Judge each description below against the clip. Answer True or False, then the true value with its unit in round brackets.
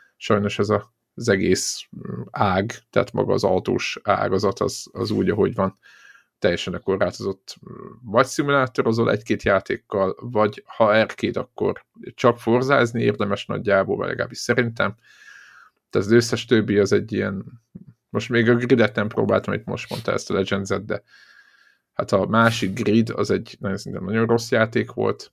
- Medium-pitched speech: False (115 Hz)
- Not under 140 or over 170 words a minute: True (155 wpm)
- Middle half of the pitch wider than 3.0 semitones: False (2.7 semitones)